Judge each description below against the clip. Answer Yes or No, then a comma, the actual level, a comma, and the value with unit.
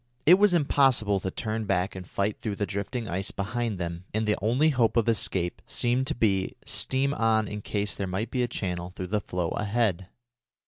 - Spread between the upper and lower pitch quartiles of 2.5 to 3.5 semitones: No, average, 4.0 semitones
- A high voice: No, low, 105 Hz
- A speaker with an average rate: No, fast, 210 wpm